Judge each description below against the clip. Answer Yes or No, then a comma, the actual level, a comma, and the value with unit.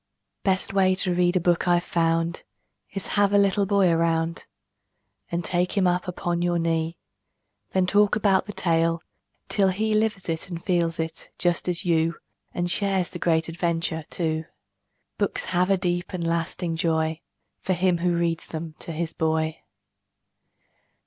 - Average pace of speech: Yes, average, 160 wpm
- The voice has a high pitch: No, medium, 175 Hz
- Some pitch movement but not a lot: No, narrow, 2.0 semitones